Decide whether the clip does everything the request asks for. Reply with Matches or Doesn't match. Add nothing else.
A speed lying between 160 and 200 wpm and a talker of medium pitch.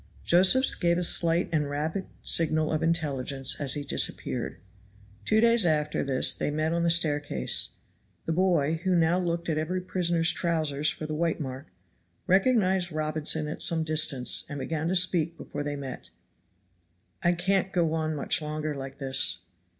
Matches